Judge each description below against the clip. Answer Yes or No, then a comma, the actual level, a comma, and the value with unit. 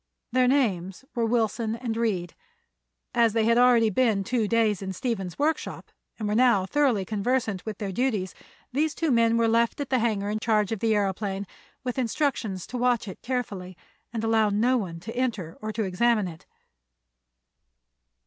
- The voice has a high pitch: Yes, high, 225 Hz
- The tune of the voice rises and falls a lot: No, average, 3.4 semitones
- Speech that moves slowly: No, average, 175 wpm